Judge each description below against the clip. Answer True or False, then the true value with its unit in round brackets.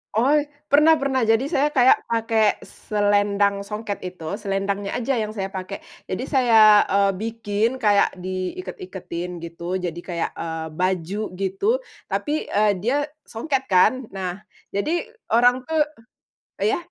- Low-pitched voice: False (205 Hz)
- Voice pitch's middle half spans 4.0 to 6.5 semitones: True (4.3 semitones)